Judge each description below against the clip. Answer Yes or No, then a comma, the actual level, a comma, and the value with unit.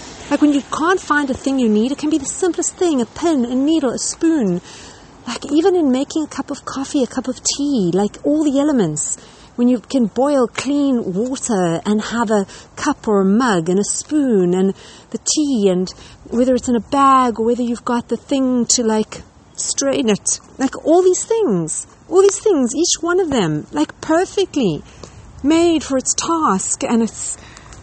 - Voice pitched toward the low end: No, very high, 260 Hz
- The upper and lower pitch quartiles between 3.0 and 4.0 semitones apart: No, average, 5.3 semitones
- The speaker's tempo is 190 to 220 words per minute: Yes, average, 195 wpm